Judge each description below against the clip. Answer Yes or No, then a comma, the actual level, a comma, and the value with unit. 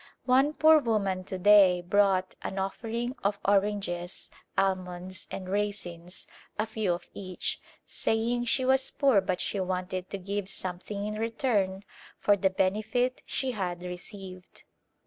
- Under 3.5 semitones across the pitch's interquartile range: Yes, average, 3.1 semitones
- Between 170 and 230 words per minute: No, average, 145 wpm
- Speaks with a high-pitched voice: Yes, high, 195 Hz